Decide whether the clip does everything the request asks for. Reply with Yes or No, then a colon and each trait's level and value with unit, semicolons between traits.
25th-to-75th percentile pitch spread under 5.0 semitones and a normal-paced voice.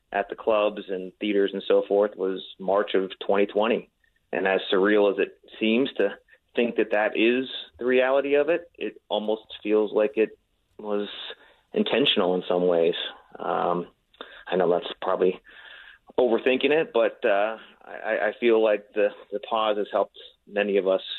Yes: average, 3.9 semitones; average, 165 wpm